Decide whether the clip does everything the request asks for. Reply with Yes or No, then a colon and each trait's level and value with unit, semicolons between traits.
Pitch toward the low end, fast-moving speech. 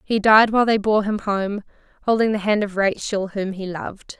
No: high, 205 Hz; fast, 215 wpm